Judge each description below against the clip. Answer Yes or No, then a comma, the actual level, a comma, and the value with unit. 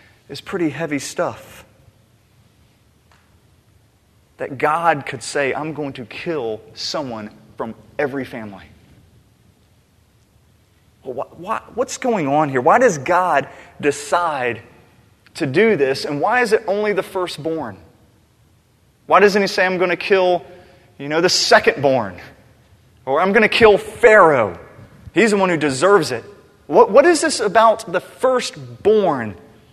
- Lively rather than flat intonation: Yes, wide, 8.1 semitones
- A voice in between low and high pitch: Yes, medium, 150 Hz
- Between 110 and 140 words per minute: Yes, slow, 135 wpm